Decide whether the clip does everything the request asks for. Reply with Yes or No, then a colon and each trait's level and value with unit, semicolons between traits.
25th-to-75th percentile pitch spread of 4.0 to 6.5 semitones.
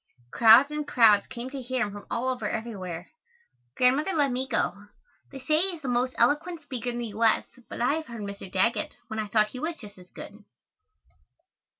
Yes: average, 4.4 semitones